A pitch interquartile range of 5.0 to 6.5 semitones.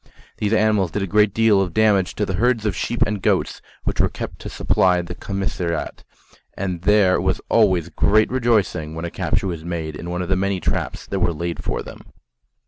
No: average, 3.4 semitones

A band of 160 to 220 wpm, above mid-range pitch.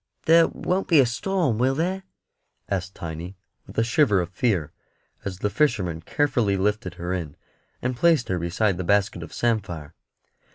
No: average, 165 wpm; low, 105 Hz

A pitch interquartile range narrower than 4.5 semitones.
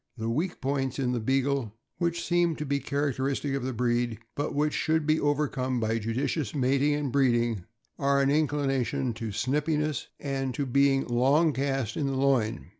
Yes: average, 2.9 semitones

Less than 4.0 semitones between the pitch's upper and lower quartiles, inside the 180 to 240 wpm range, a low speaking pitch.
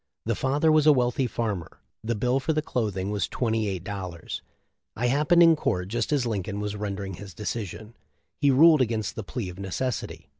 No: average, 4.8 semitones; average, 190 wpm; low, 110 Hz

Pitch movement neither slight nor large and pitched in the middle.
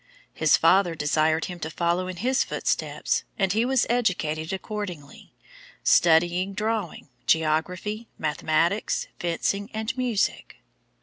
Yes: average, 4.8 semitones; medium, 180 Hz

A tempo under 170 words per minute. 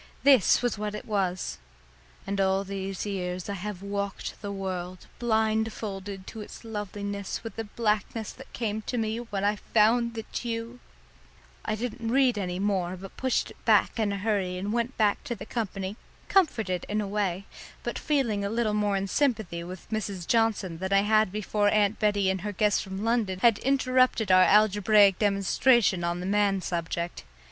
No: average, 185 wpm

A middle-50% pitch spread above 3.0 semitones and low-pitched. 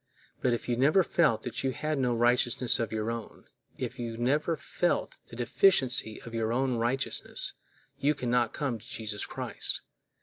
No: narrow, 2.6 semitones; low, 120 Hz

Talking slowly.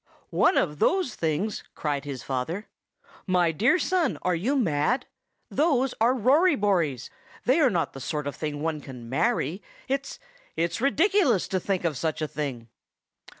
No: average, 155 wpm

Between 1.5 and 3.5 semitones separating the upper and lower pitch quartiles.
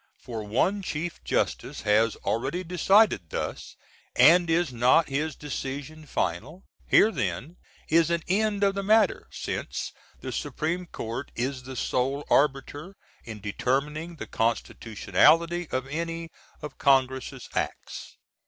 No: average, 5.1 semitones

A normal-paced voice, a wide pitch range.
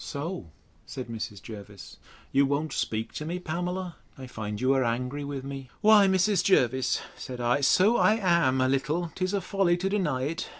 Yes: average, 185 wpm; wide, 6.0 semitones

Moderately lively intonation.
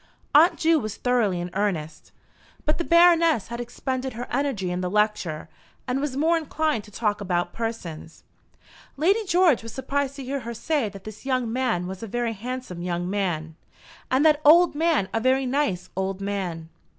No: wide, 6.8 semitones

